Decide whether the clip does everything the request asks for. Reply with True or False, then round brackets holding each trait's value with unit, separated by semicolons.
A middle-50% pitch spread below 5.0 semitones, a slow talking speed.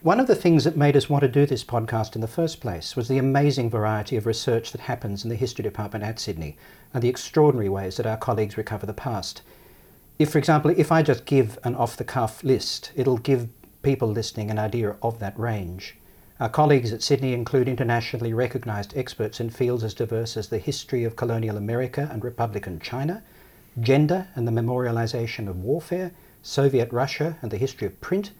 False (3.8 semitones; 200 wpm)